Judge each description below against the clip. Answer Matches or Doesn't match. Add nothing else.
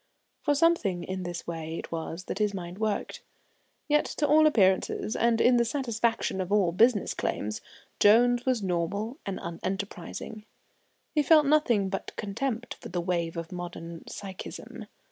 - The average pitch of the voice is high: Matches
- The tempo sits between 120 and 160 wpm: Matches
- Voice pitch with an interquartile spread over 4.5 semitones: Matches